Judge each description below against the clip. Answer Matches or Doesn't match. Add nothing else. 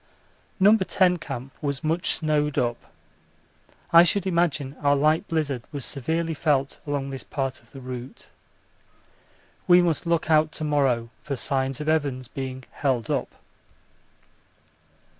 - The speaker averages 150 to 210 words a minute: Doesn't match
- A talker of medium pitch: Matches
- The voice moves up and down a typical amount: Matches